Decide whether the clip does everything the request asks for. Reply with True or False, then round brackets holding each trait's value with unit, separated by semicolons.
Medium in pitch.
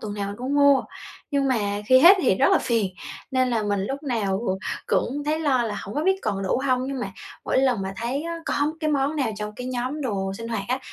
False (255 Hz)